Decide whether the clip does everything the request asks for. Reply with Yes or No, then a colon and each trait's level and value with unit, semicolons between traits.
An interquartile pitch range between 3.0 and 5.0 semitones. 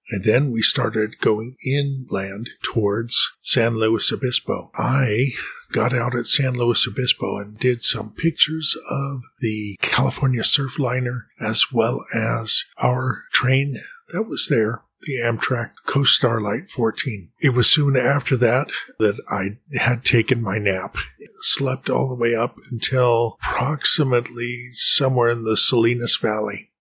No: narrow, 2.6 semitones